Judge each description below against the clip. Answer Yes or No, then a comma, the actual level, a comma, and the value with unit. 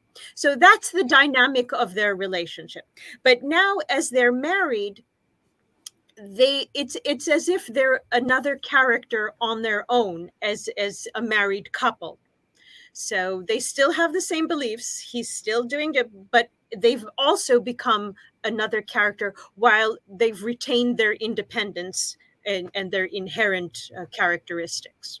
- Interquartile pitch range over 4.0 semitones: Yes, average, 4.4 semitones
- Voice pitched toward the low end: No, high, 230 Hz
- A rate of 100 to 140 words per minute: Yes, slow, 135 wpm